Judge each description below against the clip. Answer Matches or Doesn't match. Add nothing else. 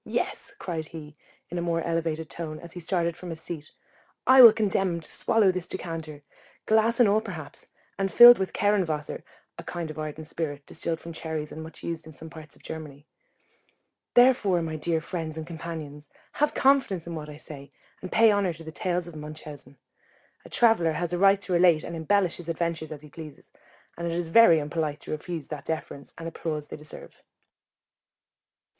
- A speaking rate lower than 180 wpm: Doesn't match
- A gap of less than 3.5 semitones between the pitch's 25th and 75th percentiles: Matches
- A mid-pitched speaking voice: Matches